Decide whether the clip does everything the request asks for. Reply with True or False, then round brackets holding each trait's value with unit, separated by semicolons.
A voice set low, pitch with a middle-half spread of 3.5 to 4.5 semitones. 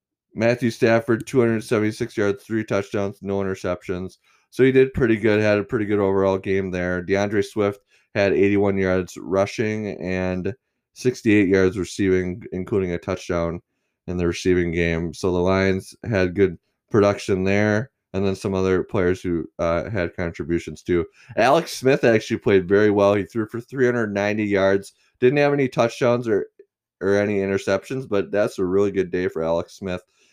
False (100 Hz; 3.1 semitones)